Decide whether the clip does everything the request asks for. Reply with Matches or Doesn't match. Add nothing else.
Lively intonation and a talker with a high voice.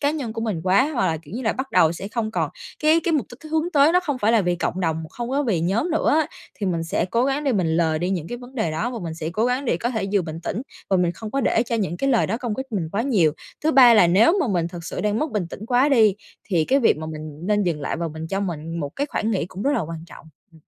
Matches